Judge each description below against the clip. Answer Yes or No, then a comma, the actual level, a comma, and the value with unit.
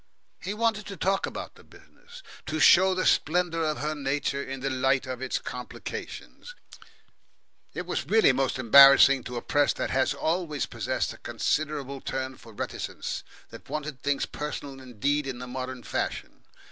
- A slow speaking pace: No, average, 165 wpm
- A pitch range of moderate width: Yes, average, 3.2 semitones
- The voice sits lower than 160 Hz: Yes, medium, 140 Hz